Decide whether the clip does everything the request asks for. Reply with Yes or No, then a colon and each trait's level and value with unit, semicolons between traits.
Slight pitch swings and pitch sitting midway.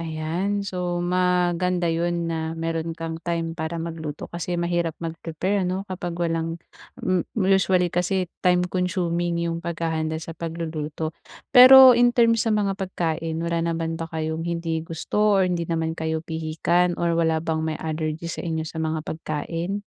Yes: narrow, 1.8 semitones; medium, 170 Hz